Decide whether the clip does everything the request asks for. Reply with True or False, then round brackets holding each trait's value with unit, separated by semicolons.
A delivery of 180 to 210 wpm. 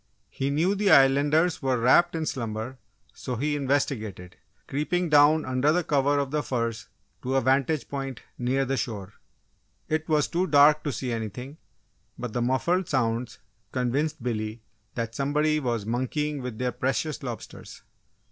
False (150 wpm)